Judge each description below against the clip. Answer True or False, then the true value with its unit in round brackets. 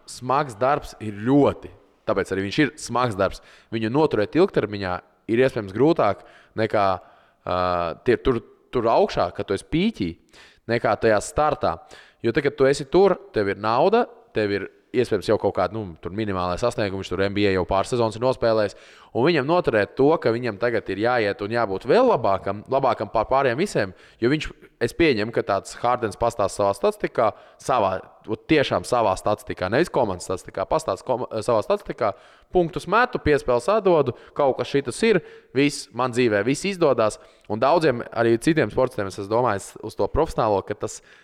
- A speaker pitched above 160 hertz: False (115 Hz)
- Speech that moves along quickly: False (165 wpm)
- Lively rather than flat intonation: True (6.0 semitones)